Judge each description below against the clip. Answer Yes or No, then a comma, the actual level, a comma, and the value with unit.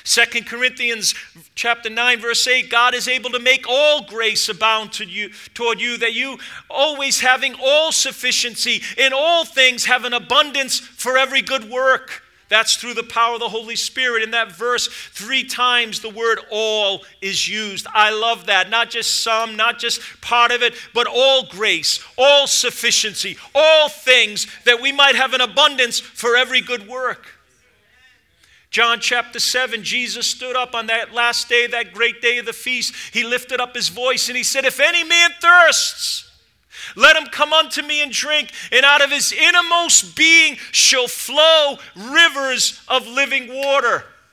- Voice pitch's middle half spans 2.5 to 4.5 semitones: Yes, average, 2.8 semitones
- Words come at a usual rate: Yes, average, 170 wpm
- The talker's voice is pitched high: Yes, high, 245 Hz